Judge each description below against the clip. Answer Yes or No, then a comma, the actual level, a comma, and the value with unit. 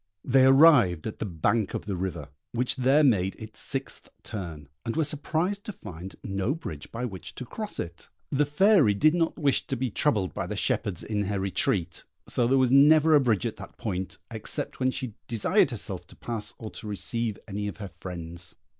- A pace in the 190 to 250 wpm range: Yes, average, 200 wpm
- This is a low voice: Yes, low, 110 Hz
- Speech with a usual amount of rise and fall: No, wide, 6.2 semitones